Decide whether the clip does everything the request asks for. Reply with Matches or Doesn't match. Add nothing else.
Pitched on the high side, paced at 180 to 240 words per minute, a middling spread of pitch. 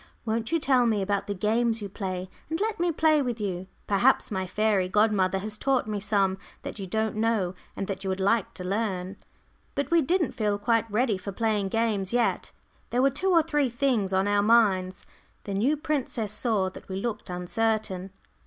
Matches